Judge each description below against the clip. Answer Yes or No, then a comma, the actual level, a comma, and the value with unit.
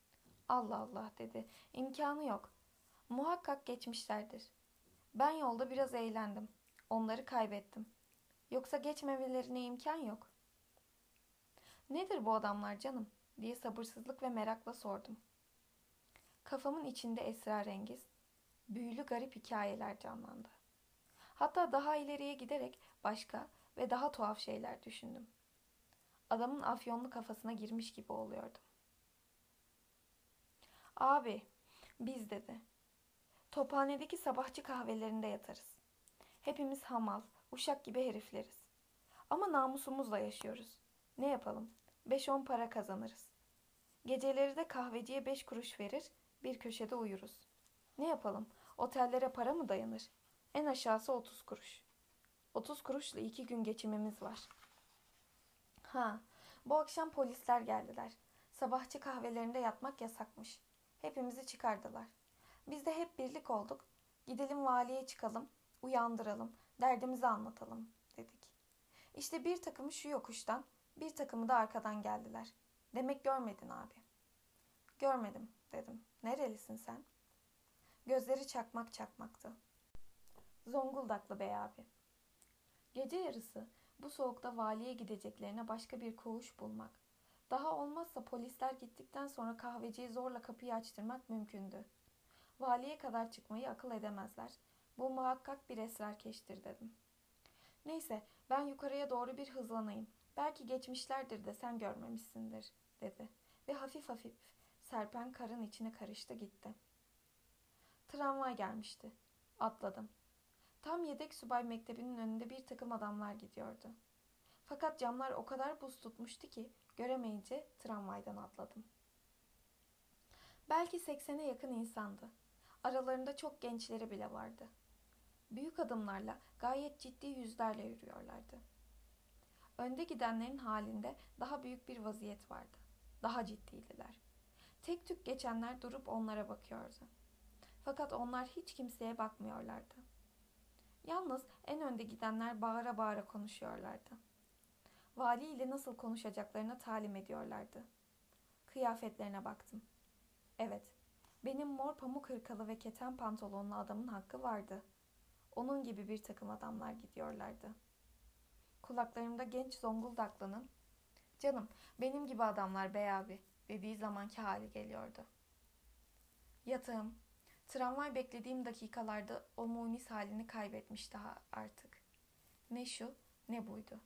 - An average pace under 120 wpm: Yes, average, 105 wpm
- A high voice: Yes, high, 235 Hz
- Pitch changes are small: No, average, 3.6 semitones